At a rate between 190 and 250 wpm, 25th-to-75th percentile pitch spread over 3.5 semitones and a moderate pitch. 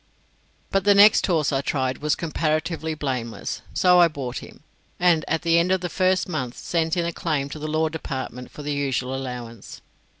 Yes: average, 195 wpm; average, 4.1 semitones; medium, 155 Hz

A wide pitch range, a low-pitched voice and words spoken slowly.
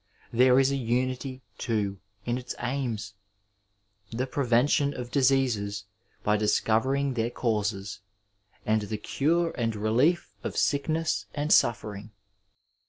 No: average, 4.1 semitones; low, 120 Hz; slow, 120 wpm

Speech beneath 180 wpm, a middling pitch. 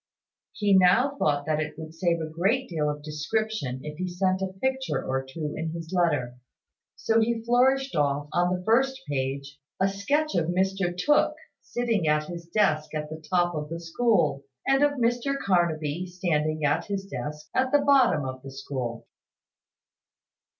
Yes: average, 170 wpm; medium, 175 Hz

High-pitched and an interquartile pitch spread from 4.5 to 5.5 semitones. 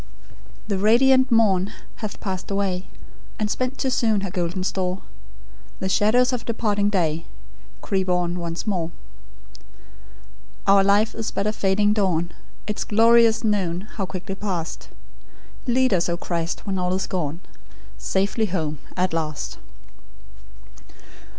No: high, 195 Hz; average, 3.1 semitones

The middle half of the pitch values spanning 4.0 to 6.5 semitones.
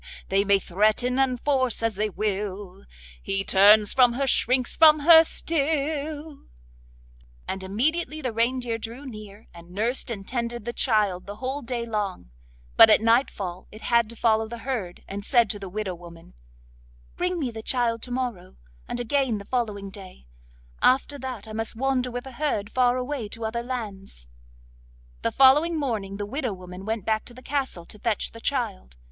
Yes: average, 4.3 semitones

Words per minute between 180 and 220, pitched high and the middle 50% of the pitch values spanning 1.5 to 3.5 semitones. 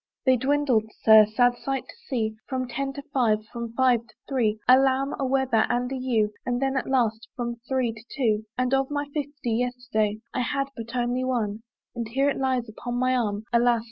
Yes: fast, 205 wpm; high, 245 Hz; narrow, 2.6 semitones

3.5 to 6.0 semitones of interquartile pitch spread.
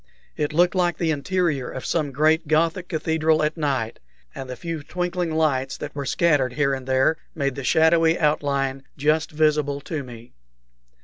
No: average, 2.9 semitones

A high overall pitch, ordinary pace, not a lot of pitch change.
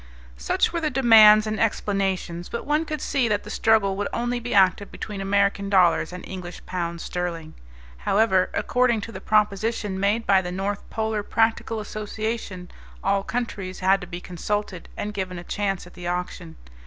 No: high, 200 Hz; average, 175 wpm; average, 3.2 semitones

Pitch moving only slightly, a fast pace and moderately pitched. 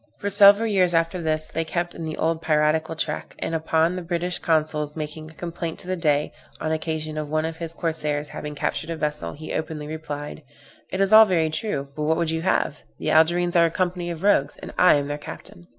Yes: narrow, 2.1 semitones; fast, 225 wpm; medium, 160 Hz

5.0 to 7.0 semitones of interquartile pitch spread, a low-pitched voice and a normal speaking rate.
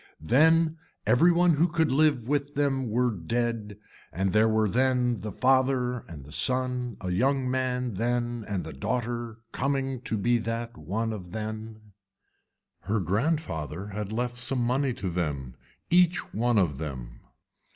No: average, 4.0 semitones; low, 120 Hz; average, 150 wpm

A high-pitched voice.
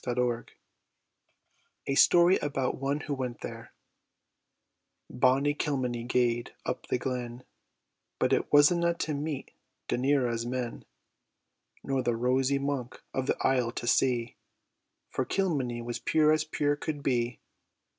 No: low, 130 Hz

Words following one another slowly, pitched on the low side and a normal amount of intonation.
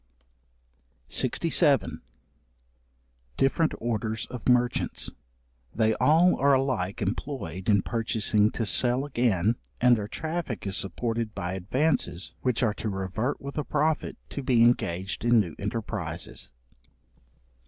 Yes: slow, 120 wpm; low, 115 Hz; average, 4.4 semitones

